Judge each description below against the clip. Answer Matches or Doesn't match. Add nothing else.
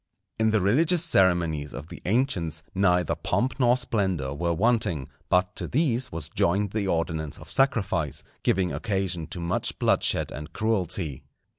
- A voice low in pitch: Matches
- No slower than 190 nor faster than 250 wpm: Doesn't match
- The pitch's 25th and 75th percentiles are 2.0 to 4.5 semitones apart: Doesn't match